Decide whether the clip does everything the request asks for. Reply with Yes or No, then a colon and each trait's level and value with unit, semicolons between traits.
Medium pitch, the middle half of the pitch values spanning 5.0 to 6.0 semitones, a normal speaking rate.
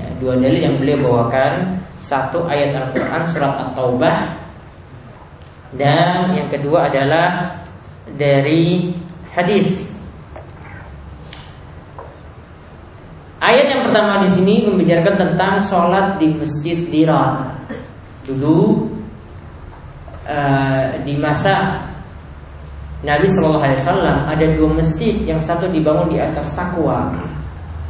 Yes: medium, 150 Hz; wide, 5.5 semitones; average, 95 wpm